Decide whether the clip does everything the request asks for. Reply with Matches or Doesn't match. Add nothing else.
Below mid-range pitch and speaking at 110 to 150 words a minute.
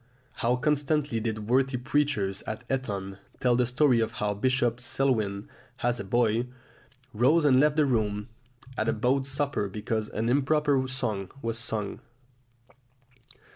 Matches